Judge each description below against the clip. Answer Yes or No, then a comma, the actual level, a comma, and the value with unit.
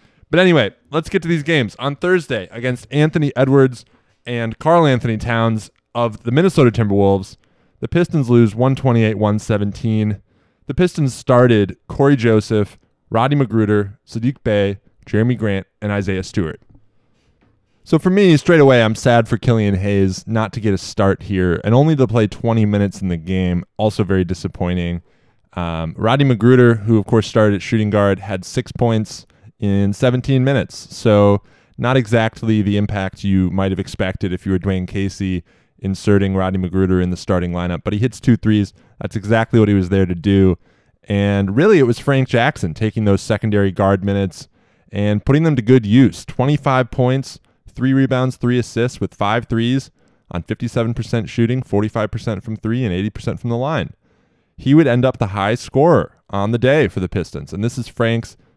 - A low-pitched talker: Yes, low, 110 Hz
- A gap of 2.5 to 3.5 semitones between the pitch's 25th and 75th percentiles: No, average, 4.2 semitones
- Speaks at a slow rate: No, average, 175 wpm